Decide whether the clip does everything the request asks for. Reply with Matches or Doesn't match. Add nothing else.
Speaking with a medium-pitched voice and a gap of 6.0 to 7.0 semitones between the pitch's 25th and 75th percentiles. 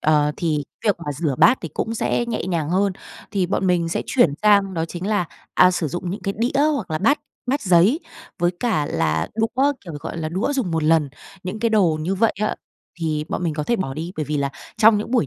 Doesn't match